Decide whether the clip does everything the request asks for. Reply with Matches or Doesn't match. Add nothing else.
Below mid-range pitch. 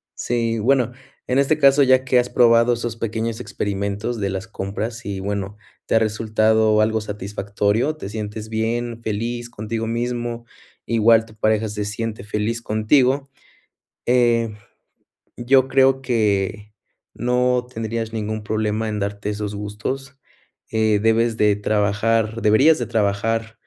Matches